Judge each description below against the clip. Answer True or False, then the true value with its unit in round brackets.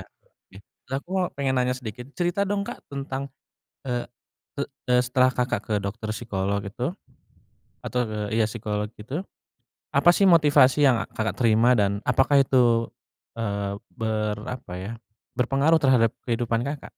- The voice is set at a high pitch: False (125 Hz)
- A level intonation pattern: False (3.9 semitones)